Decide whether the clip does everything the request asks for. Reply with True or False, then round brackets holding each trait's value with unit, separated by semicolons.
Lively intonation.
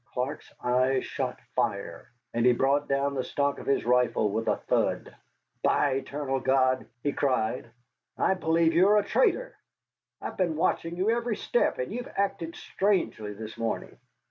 True (6.3 semitones)